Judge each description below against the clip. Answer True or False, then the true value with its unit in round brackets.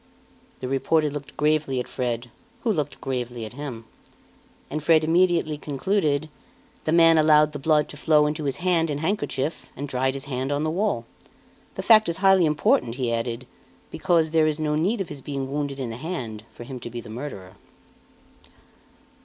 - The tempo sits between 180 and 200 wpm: True (185 wpm)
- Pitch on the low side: False (150 Hz)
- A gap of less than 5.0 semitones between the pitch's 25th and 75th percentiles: True (3.6 semitones)